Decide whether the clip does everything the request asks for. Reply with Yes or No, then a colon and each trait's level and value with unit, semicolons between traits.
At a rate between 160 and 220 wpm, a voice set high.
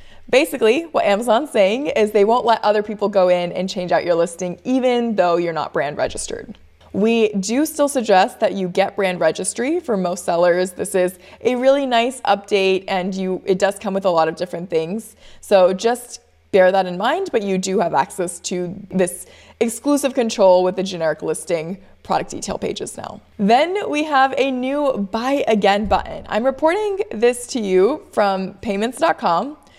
Yes: average, 180 wpm; high, 200 Hz